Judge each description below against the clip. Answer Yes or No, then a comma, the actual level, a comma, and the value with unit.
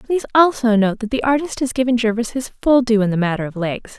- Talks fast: Yes, fast, 255 wpm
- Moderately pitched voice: No, high, 235 Hz